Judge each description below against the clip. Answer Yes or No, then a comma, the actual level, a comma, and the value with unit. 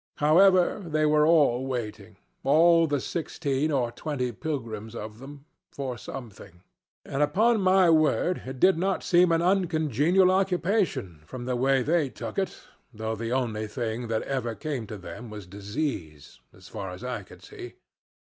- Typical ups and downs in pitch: No, wide, 6.6 semitones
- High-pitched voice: No, low, 135 Hz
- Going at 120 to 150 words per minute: No, average, 160 wpm